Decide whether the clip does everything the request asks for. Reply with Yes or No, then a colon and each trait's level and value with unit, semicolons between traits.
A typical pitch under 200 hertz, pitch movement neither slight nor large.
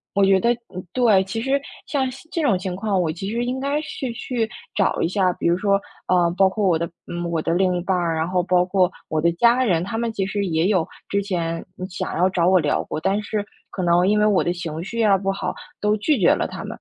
Yes: high, 190 Hz; average, 3.5 semitones